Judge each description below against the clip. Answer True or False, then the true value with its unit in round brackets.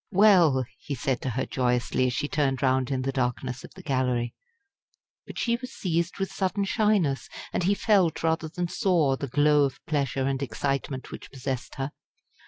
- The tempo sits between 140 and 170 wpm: False (185 wpm)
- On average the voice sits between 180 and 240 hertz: False (140 Hz)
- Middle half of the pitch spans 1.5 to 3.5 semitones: False (4.9 semitones)